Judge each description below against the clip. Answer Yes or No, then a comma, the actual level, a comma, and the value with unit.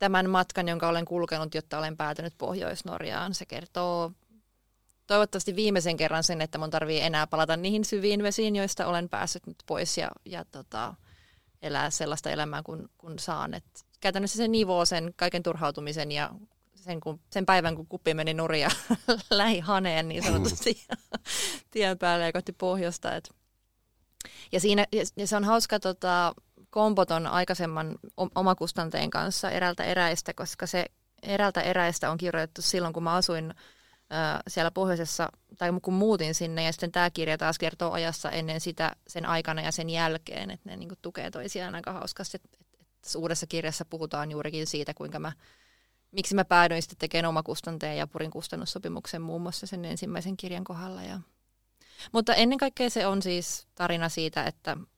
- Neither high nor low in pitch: Yes, medium, 170 Hz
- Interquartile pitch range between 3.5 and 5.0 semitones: No, average, 2.8 semitones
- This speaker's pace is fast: Yes, fast, 160 wpm